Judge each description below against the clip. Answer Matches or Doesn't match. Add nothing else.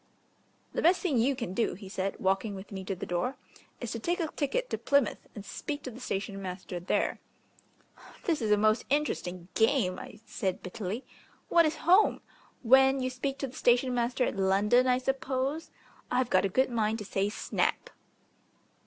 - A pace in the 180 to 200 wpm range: Matches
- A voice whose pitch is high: Matches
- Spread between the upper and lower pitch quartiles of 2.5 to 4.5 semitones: Doesn't match